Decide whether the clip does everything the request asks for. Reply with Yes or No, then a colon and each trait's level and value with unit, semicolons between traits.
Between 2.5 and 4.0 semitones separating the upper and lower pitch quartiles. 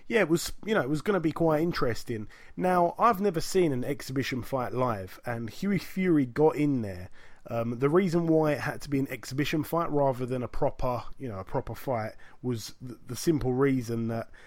No: average, 4.9 semitones